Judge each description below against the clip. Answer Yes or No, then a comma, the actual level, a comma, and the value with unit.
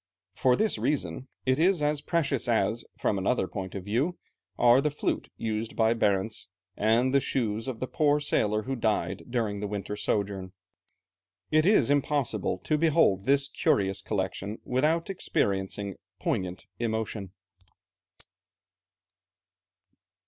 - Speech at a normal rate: No, slow, 130 wpm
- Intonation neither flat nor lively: No, wide, 5.7 semitones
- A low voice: Yes, low, 115 Hz